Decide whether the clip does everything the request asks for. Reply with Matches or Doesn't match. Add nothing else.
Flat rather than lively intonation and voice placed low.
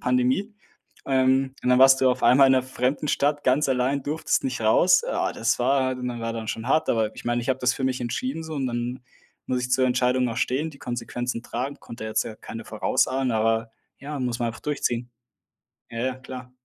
Matches